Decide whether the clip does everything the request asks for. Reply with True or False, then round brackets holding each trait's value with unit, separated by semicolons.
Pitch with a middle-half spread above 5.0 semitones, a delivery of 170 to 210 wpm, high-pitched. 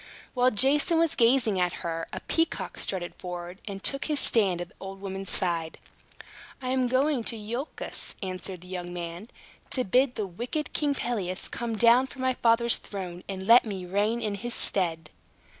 True (5.5 semitones; 180 wpm; 210 Hz)